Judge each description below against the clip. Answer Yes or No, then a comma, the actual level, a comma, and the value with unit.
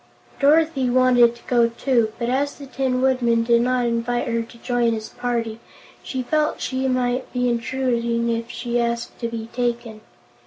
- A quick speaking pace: No, average, 170 wpm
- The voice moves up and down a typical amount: No, narrow, 1.6 semitones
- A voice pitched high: Yes, high, 245 Hz